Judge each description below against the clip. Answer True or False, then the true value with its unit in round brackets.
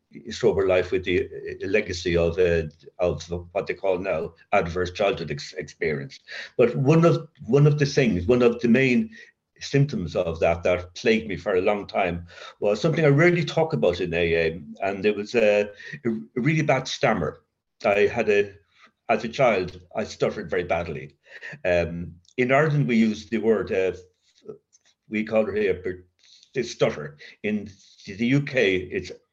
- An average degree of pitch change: False (8.6 semitones)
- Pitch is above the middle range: False (110 Hz)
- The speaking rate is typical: True (165 wpm)